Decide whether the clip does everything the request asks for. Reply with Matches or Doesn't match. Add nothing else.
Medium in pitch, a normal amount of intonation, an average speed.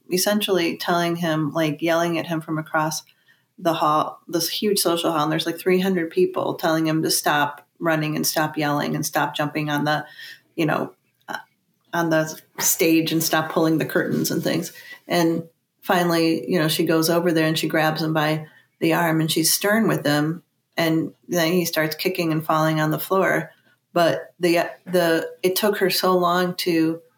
Doesn't match